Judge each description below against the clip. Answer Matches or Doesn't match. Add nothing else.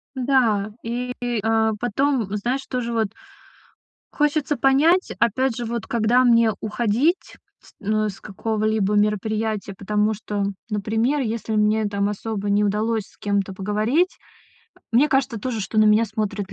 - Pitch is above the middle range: Matches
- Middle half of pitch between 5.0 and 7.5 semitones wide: Doesn't match